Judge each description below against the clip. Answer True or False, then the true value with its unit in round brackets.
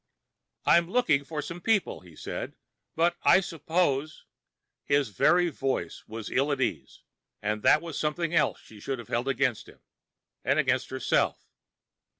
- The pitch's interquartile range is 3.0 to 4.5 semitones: False (5.1 semitones)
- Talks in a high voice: False (145 Hz)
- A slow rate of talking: False (155 wpm)